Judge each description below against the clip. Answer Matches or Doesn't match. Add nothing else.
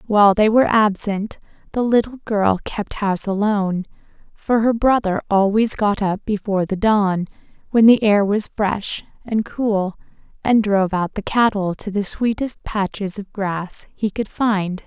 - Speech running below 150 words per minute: Doesn't match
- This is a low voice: Doesn't match